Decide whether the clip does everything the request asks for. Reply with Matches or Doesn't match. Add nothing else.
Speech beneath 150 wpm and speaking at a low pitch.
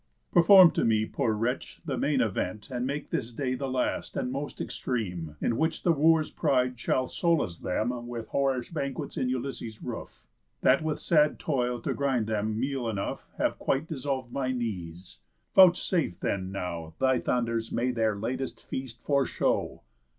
Doesn't match